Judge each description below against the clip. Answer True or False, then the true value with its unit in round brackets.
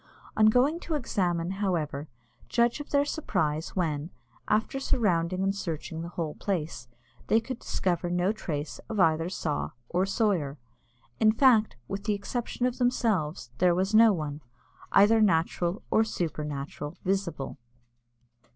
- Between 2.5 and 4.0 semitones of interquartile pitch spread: False (5.4 semitones)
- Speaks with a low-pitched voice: False (185 Hz)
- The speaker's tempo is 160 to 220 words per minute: False (140 wpm)